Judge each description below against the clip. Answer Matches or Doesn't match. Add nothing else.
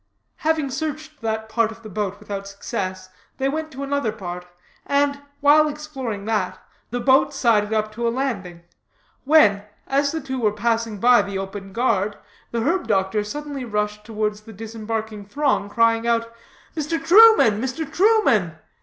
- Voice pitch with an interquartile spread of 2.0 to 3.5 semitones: Doesn't match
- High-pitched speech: Matches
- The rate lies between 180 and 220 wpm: Doesn't match